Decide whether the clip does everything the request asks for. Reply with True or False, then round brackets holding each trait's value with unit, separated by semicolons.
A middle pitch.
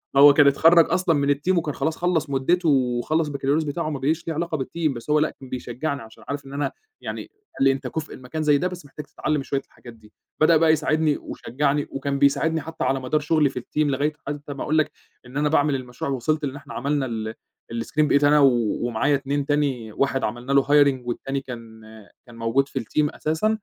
True (145 Hz)